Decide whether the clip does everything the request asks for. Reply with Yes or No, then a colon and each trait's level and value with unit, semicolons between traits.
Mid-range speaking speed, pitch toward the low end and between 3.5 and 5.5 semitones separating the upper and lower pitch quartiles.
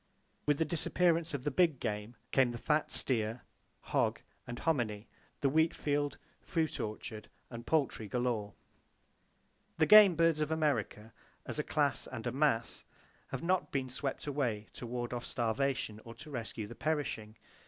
Yes: average, 160 wpm; low, 130 Hz; average, 5.1 semitones